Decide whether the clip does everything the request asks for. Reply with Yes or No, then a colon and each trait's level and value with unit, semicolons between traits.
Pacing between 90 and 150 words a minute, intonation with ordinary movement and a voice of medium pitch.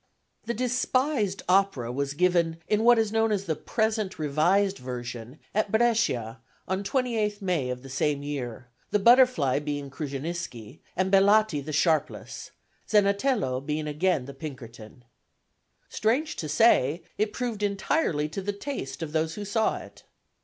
No: average, 145 wpm; wide, 7.2 semitones; medium, 180 Hz